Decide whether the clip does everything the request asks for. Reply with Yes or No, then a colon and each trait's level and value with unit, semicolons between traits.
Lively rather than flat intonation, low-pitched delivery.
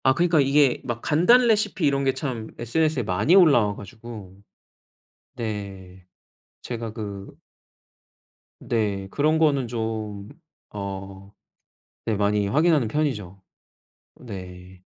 Yes: wide, 6.2 semitones; low, 115 Hz